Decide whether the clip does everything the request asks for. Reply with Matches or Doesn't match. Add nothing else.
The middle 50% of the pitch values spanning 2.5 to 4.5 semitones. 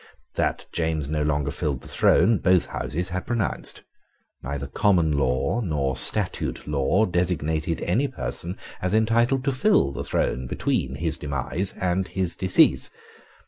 Doesn't match